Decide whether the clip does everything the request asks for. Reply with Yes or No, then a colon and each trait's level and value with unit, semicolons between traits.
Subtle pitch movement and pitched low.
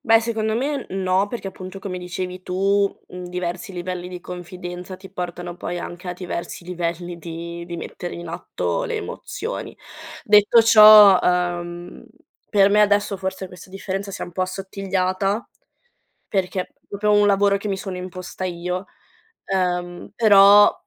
No: narrow, 2.1 semitones; medium, 185 Hz